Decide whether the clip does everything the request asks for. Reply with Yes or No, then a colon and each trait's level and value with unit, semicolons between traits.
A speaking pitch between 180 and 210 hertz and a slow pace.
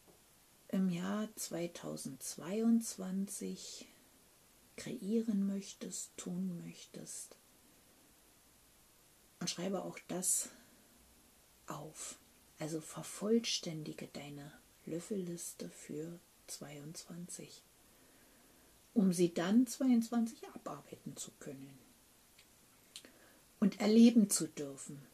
Yes: medium, 185 Hz; slow, 70 wpm